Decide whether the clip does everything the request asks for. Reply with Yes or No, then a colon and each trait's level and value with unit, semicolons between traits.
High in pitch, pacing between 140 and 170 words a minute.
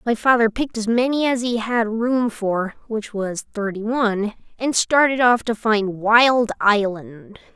Yes: high, 225 Hz; average, 165 wpm